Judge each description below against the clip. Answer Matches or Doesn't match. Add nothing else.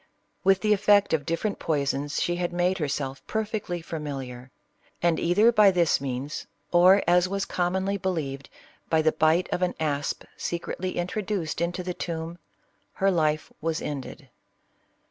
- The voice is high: Doesn't match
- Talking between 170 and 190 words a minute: Doesn't match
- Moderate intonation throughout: Matches